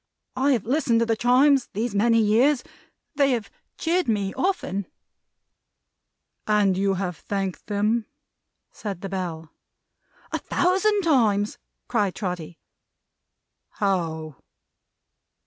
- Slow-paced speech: Yes, slow, 110 wpm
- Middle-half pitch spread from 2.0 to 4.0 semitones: No, average, 4.8 semitones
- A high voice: Yes, high, 215 Hz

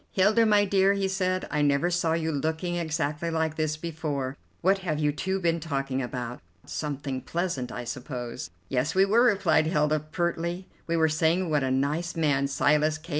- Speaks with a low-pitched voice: No, medium, 160 Hz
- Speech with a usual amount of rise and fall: Yes, average, 3.5 semitones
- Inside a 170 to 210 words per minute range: Yes, average, 180 wpm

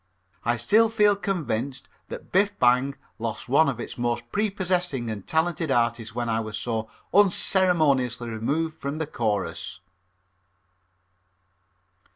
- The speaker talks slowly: Yes, slow, 125 wpm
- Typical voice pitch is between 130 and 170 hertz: Yes, low, 135 Hz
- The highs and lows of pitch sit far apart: Yes, wide, 7.1 semitones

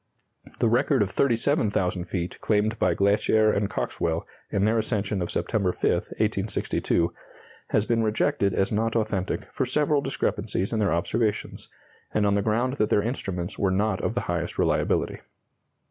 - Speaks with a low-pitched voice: Yes, low, 105 Hz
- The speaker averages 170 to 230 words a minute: No, average, 160 wpm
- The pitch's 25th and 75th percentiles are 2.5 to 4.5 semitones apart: Yes, average, 2.9 semitones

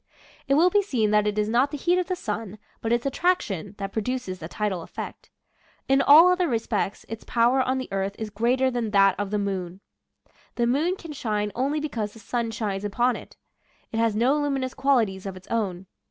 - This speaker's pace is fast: Yes, fast, 210 wpm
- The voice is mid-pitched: No, high, 230 Hz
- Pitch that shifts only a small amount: No, average, 4.7 semitones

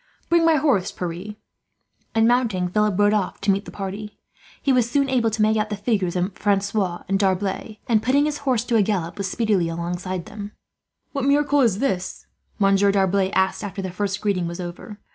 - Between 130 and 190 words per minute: No, average, 200 wpm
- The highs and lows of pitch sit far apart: No, average, 3.3 semitones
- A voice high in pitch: Yes, high, 205 Hz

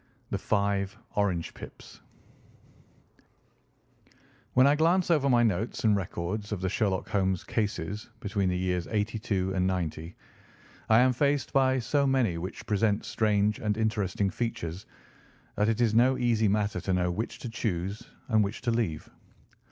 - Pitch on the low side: Yes, low, 105 Hz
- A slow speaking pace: No, average, 155 wpm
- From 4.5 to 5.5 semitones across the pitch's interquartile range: No, average, 3.8 semitones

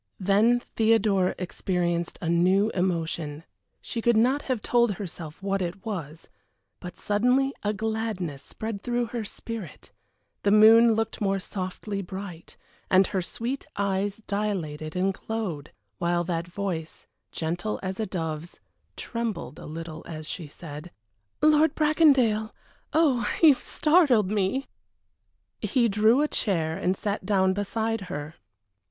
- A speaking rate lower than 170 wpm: Yes, slow, 135 wpm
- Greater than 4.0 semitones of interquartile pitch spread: Yes, average, 4.4 semitones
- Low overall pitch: No, high, 200 Hz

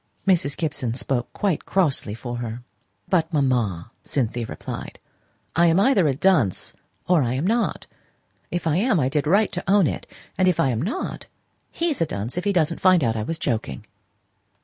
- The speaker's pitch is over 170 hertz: No, medium, 155 Hz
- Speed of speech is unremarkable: Yes, average, 180 wpm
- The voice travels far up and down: Yes, wide, 7.2 semitones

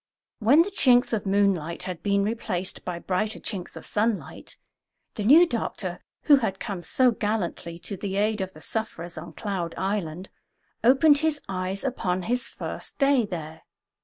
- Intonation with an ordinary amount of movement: Yes, average, 4.6 semitones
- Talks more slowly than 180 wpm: Yes, average, 160 wpm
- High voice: Yes, high, 200 Hz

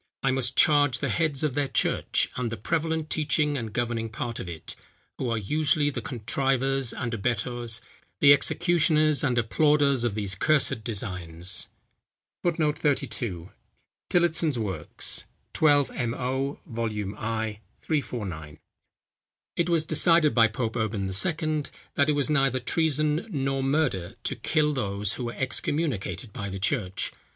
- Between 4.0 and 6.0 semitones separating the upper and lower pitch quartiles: Yes, average, 5.2 semitones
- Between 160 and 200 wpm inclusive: No, average, 140 wpm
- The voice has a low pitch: Yes, low, 130 Hz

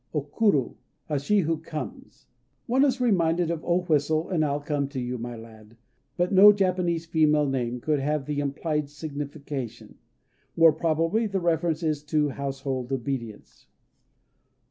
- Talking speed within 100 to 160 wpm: Yes, average, 150 wpm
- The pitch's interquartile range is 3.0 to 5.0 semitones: Yes, average, 3.6 semitones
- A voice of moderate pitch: Yes, medium, 150 Hz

